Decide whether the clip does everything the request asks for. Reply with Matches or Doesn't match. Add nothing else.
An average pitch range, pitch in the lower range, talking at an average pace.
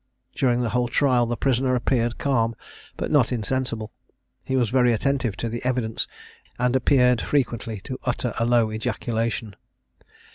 Doesn't match